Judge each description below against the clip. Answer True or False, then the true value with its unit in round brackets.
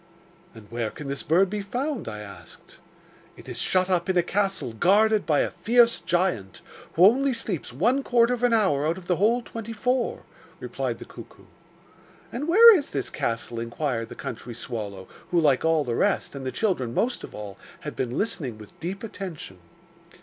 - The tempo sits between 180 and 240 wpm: True (190 wpm)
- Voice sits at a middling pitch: True (175 Hz)